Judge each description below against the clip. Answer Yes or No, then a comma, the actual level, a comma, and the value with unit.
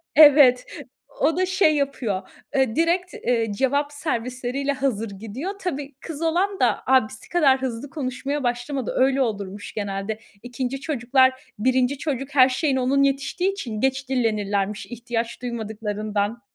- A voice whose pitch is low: No, very high, 260 Hz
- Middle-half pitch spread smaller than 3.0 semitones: No, average, 3.8 semitones